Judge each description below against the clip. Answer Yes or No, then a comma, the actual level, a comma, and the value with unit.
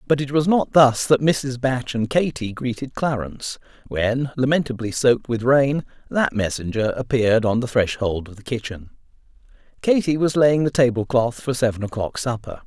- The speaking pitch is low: Yes, low, 125 Hz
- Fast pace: No, average, 170 wpm